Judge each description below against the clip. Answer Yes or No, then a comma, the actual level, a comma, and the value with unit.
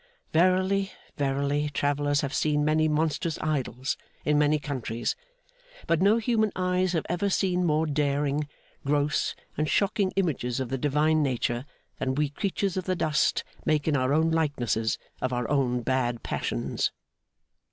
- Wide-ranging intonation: No, average, 3.5 semitones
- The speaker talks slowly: No, average, 150 wpm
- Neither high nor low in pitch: Yes, medium, 150 Hz